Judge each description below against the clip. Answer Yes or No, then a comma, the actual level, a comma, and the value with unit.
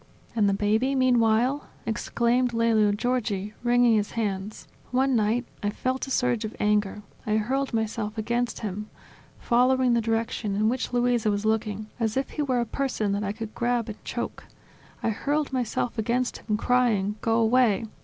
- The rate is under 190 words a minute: Yes, average, 170 wpm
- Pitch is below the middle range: No, high, 230 Hz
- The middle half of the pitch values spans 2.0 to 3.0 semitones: Yes, average, 2.7 semitones